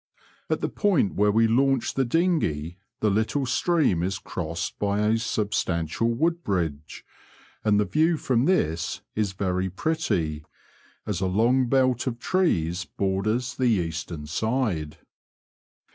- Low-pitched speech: Yes, low, 105 Hz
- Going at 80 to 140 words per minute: Yes, slow, 135 wpm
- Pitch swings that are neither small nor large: No, wide, 6.6 semitones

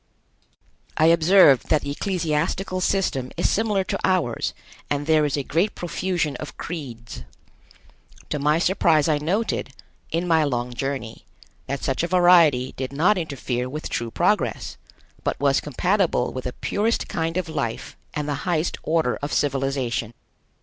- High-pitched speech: No, medium, 150 Hz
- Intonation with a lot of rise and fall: No, average, 4.5 semitones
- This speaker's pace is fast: No, average, 150 wpm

